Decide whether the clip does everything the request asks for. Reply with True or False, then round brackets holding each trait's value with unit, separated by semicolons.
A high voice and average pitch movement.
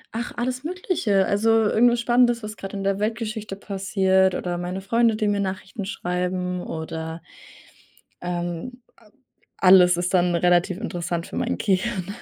True (195 Hz; 3.9 semitones)